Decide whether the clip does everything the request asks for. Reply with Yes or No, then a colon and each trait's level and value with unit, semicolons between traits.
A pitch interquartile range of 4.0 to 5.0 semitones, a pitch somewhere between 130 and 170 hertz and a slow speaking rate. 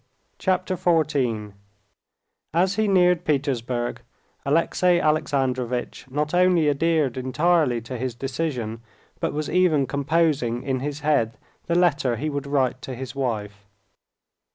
Yes: average, 4.6 semitones; medium, 140 Hz; slow, 125 wpm